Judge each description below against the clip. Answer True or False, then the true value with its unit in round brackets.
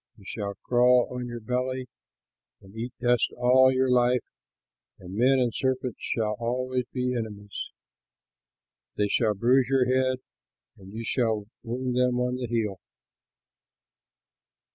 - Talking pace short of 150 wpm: True (135 wpm)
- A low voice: True (125 Hz)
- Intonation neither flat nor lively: False (2.2 semitones)